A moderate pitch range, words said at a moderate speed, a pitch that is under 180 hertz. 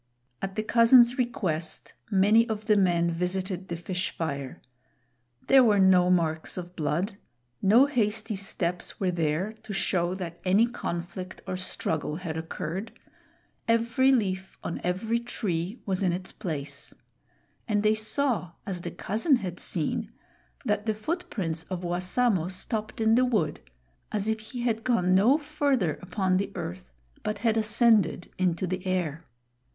No: average, 4.1 semitones; average, 150 wpm; high, 190 Hz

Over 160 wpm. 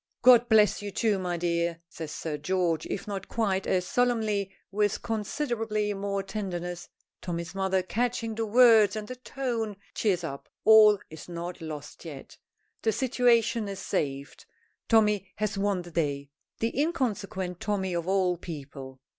No: average, 150 wpm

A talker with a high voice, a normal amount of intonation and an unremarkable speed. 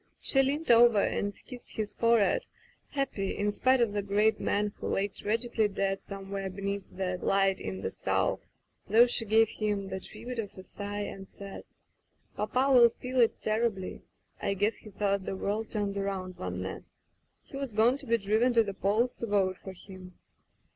Yes: high, 205 Hz; average, 3.0 semitones; average, 185 wpm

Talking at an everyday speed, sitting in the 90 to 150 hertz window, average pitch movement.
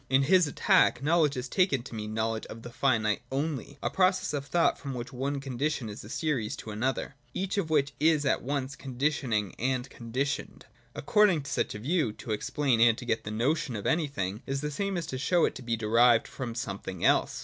No: fast, 210 wpm; low, 135 Hz; average, 4.5 semitones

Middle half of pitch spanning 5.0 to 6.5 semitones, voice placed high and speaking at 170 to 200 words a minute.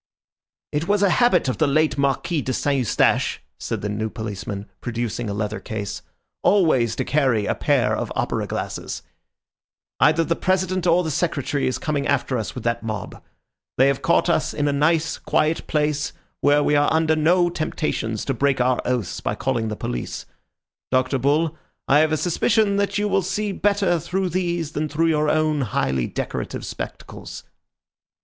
No: average, 5.3 semitones; medium, 150 Hz; average, 175 wpm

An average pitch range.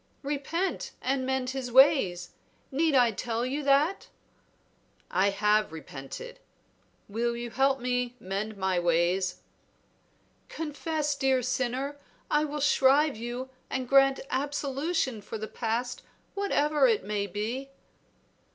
Yes: average, 4.7 semitones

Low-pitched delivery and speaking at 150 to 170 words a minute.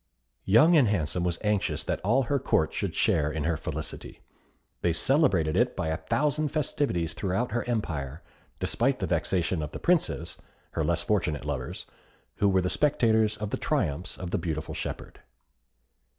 Yes: very low, 90 Hz; average, 165 wpm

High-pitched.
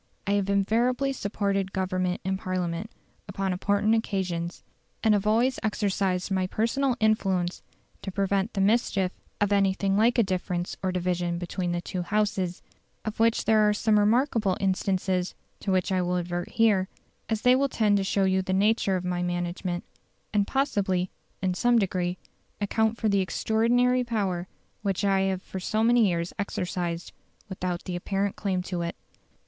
Yes: high, 195 Hz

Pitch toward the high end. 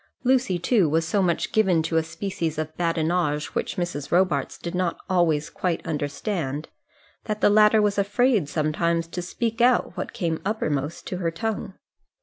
No: medium, 175 Hz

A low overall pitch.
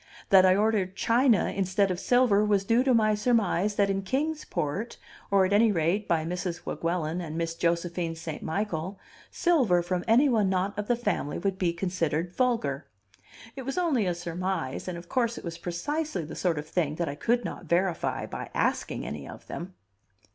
No: high, 190 Hz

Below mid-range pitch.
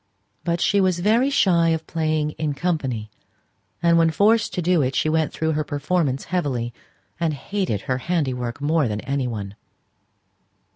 No: medium, 155 Hz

